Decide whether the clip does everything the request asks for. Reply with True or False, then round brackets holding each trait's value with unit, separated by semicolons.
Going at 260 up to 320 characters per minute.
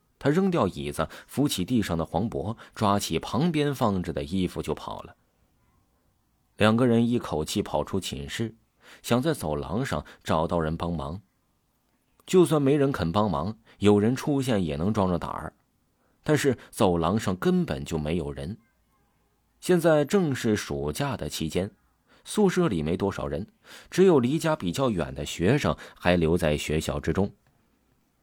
False (225 characters per minute)